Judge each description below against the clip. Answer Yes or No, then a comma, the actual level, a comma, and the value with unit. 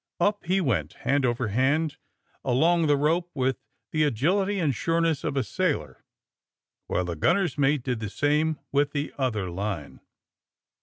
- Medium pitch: Yes, medium, 145 Hz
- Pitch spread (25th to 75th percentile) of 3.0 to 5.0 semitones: No, wide, 5.4 semitones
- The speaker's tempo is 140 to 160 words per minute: Yes, average, 155 wpm